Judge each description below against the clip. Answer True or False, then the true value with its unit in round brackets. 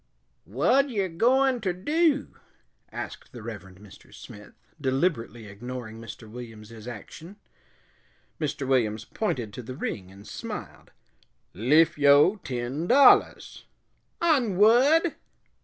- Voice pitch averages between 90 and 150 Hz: True (135 Hz)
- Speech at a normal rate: False (110 wpm)